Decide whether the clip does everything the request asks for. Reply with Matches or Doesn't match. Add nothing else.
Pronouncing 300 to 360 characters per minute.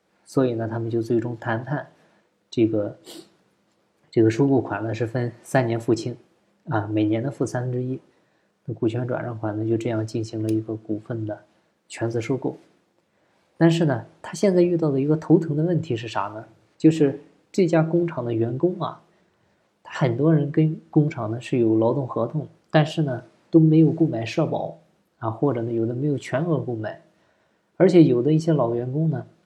Doesn't match